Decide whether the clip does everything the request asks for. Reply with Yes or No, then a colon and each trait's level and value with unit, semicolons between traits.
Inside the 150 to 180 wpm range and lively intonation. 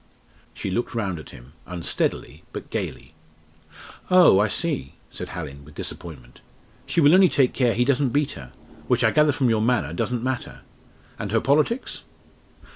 Yes: average, 170 wpm; wide, 8.7 semitones